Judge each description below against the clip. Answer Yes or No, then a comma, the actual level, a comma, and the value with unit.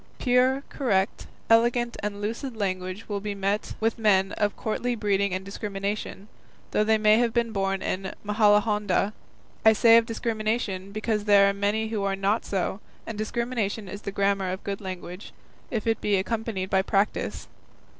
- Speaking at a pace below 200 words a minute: Yes, average, 170 wpm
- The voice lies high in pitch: Yes, high, 210 Hz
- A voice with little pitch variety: Yes, narrow, 2.3 semitones